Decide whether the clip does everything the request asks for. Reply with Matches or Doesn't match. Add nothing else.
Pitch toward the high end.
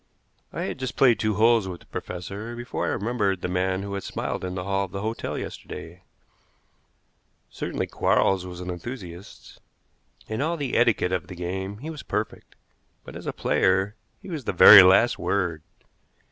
Doesn't match